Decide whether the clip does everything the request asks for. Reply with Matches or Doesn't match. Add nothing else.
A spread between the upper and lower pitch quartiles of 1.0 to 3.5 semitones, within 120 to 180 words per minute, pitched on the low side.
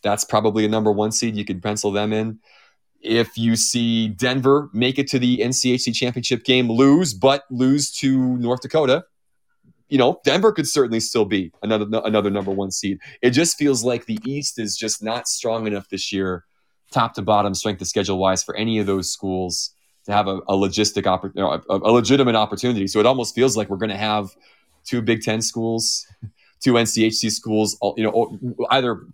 Doesn't match